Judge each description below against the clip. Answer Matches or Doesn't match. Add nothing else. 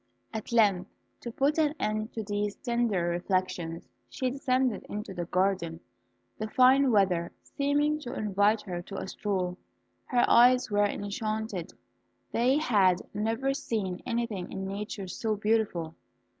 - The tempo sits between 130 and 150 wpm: Matches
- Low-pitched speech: Doesn't match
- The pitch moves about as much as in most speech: Matches